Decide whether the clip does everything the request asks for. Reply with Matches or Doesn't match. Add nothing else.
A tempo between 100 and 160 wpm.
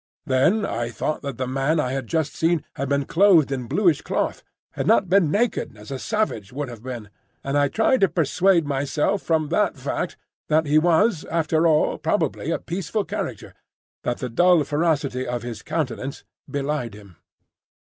Doesn't match